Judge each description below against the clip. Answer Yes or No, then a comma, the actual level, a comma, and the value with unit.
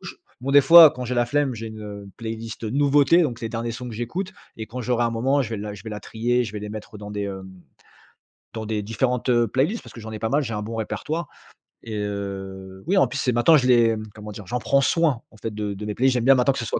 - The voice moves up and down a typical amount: Yes, average, 3.5 semitones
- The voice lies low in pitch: Yes, low, 115 Hz